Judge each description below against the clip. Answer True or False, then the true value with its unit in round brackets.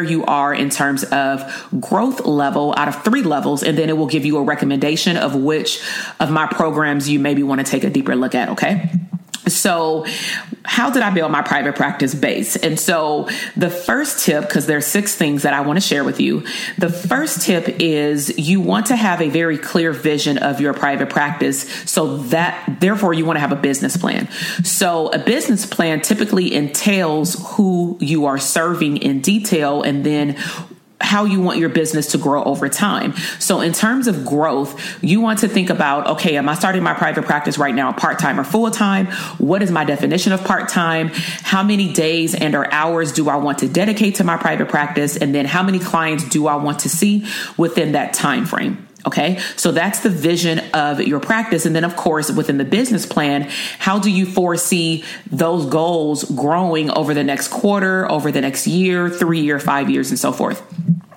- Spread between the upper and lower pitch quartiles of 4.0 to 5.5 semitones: True (4.6 semitones)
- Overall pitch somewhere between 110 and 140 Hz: False (165 Hz)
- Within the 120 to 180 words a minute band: False (200 wpm)